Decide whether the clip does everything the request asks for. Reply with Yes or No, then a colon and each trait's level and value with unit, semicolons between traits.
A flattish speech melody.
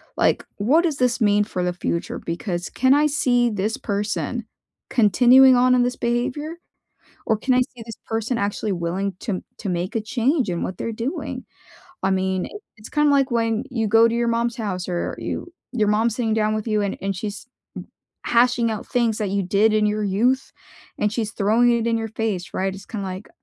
No: average, 3.3 semitones